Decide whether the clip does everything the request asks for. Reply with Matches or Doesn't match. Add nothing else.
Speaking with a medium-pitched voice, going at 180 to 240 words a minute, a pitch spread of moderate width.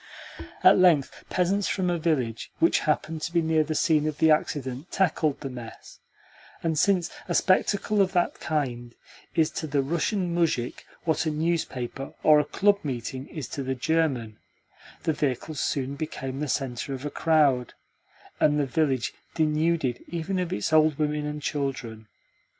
Doesn't match